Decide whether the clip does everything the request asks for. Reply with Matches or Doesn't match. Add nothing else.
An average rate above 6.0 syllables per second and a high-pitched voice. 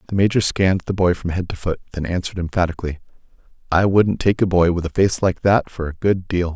Doesn't match